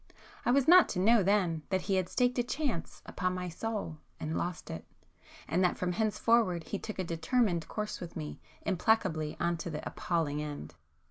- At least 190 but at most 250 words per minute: Yes, average, 195 wpm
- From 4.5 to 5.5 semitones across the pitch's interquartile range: Yes, average, 5.1 semitones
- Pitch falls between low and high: Yes, medium, 180 Hz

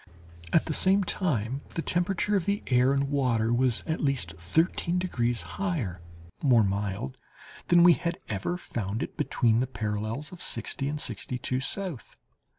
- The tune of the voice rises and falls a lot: Yes, wide, 7.3 semitones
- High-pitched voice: No, low, 135 Hz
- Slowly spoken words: No, average, 160 wpm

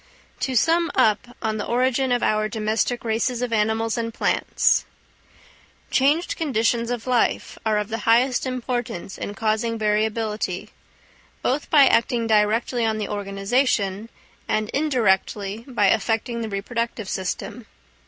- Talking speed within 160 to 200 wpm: No, slow, 135 wpm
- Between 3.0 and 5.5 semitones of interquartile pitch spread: No, narrow, 2.5 semitones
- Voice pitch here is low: No, high, 225 Hz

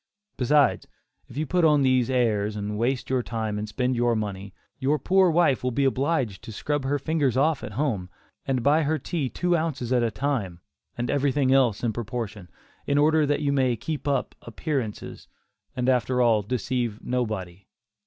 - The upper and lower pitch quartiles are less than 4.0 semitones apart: No, average, 4.4 semitones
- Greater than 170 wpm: Yes, average, 185 wpm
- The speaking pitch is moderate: No, low, 130 Hz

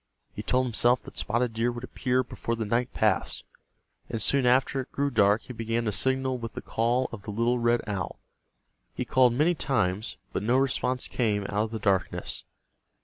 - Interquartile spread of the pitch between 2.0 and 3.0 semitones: Yes, narrow, 2.6 semitones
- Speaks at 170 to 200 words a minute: Yes, average, 195 wpm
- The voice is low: Yes, low, 120 Hz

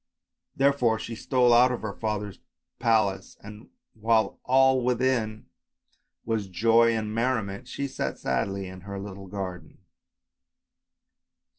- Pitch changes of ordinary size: Yes, average, 3.5 semitones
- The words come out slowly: Yes, slow, 120 wpm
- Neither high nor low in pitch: No, low, 110 Hz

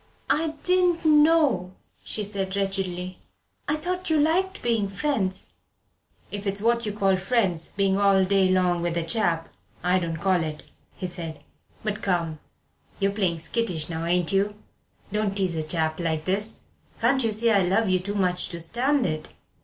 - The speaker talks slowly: No, average, 175 wpm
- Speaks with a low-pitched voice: No, high, 195 Hz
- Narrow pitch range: No, average, 4.4 semitones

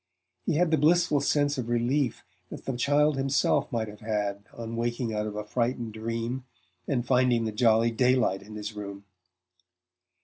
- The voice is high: No, low, 120 Hz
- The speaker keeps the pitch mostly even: No, average, 3.6 semitones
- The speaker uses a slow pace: No, average, 170 wpm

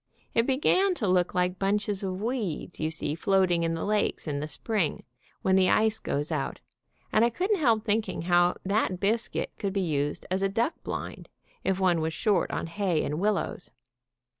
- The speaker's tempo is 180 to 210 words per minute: Yes, average, 190 wpm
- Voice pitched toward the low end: No, high, 190 Hz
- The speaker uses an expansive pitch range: No, average, 4.2 semitones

